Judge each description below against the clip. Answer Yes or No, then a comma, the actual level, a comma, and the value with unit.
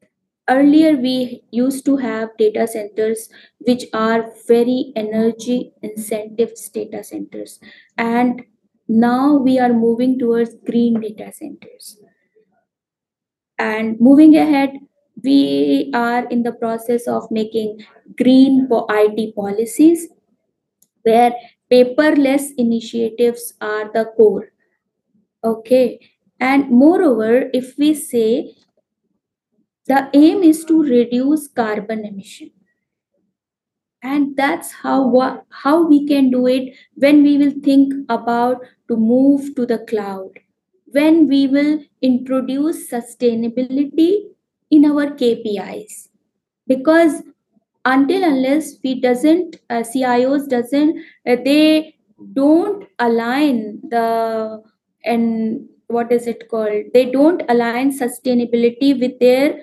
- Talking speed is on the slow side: Yes, slow, 110 wpm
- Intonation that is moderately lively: Yes, average, 3.7 semitones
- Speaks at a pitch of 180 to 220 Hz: No, high, 245 Hz